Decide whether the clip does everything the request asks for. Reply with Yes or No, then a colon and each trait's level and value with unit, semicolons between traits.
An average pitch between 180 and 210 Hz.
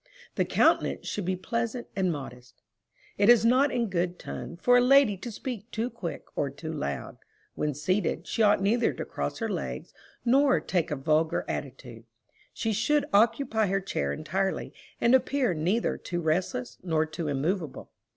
Yes: high, 190 Hz